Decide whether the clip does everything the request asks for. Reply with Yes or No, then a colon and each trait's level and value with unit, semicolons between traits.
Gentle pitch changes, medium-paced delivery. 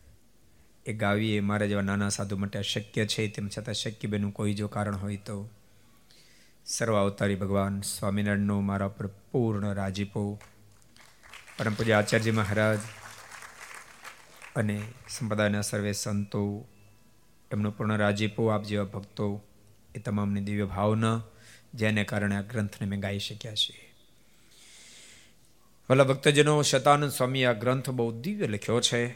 Yes: narrow, 1.8 semitones; average, 125 wpm